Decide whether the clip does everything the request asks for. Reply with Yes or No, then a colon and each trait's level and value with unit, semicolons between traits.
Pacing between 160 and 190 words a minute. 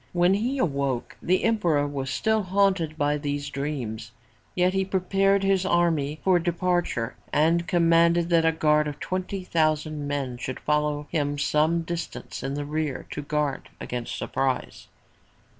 No: average, 150 wpm